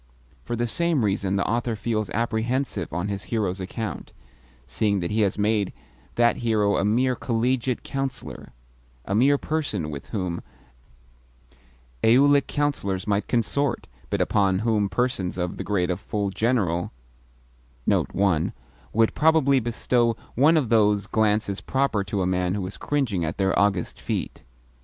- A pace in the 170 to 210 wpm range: No, average, 145 wpm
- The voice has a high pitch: No, low, 105 Hz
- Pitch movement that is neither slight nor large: Yes, average, 3.9 semitones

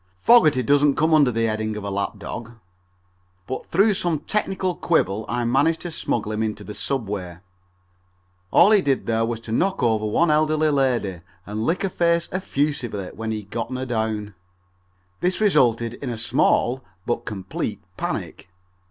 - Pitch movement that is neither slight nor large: No, wide, 6.2 semitones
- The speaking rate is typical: Yes, average, 170 wpm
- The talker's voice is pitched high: No, low, 120 Hz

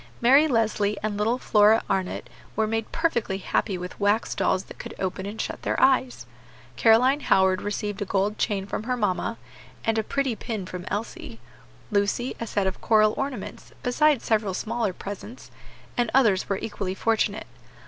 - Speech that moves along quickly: No, average, 170 wpm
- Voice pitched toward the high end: Yes, high, 215 Hz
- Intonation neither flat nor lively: Yes, average, 3.1 semitones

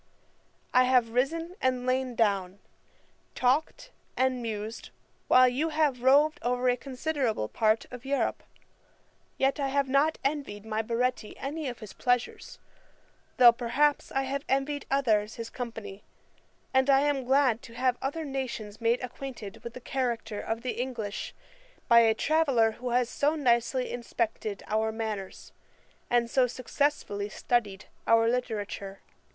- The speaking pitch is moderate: No, very high, 250 Hz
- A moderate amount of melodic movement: Yes, average, 3.2 semitones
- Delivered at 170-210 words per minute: No, average, 145 wpm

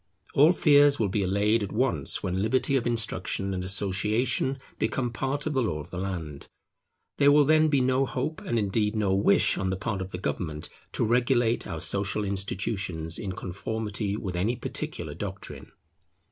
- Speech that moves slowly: No, average, 175 wpm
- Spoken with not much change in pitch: No, average, 5.0 semitones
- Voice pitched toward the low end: Yes, low, 105 Hz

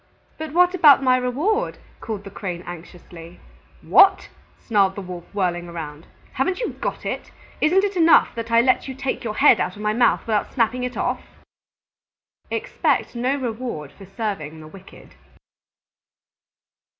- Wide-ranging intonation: Yes, wide, 6.7 semitones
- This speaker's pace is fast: No, average, 155 wpm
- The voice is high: Yes, high, 230 Hz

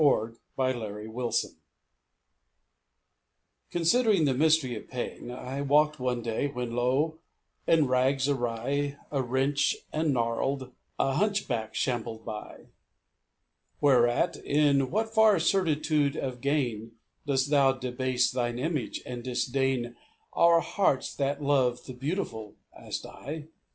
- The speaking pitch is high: No, low, 135 Hz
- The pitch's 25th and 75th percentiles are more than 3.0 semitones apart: Yes, average, 3.5 semitones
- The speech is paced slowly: Yes, slow, 125 wpm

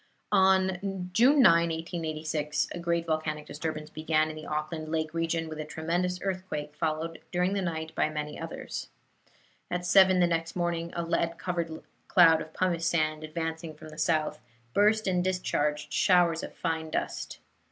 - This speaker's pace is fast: No, average, 165 wpm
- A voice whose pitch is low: No, medium, 165 Hz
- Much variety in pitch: No, narrow, 2.4 semitones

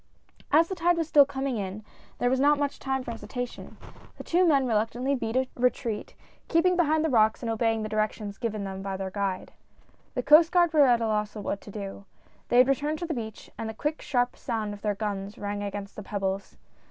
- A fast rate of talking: Yes, fast, 220 wpm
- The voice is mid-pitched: No, high, 230 Hz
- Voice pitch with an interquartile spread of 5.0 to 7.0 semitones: Yes, wide, 5.4 semitones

